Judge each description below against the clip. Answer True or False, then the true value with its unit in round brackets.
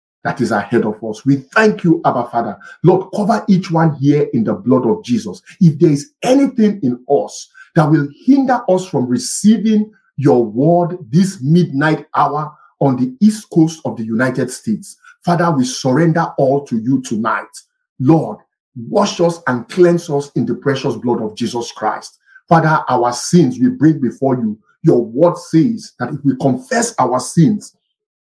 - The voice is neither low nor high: True (155 Hz)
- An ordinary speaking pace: True (170 wpm)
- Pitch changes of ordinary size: False (7.0 semitones)